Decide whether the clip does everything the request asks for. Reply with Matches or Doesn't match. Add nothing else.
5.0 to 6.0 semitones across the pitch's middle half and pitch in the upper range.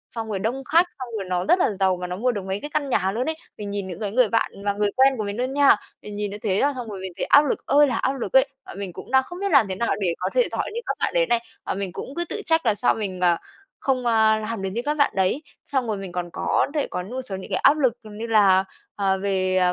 Matches